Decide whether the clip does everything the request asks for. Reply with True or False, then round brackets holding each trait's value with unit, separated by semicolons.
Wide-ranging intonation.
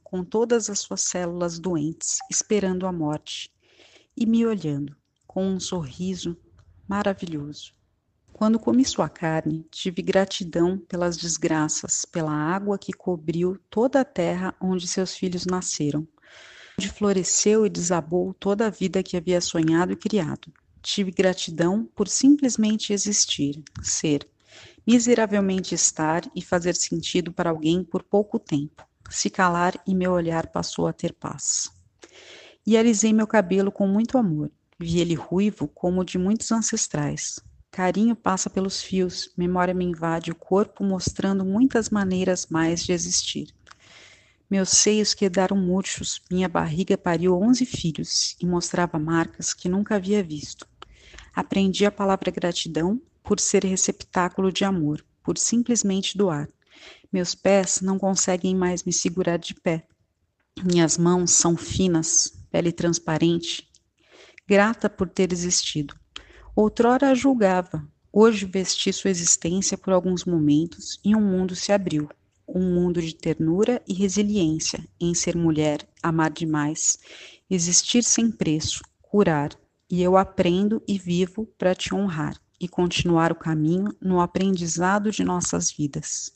False (3.1 semitones)